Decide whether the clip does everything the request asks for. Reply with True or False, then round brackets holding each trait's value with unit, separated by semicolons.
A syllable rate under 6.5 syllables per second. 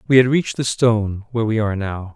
False (6.8 syllables/s)